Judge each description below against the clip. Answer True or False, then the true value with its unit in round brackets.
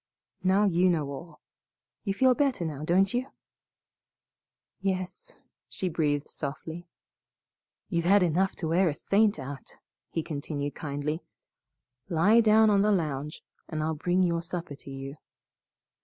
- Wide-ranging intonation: False (4.3 semitones)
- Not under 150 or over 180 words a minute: False (140 wpm)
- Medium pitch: True (170 Hz)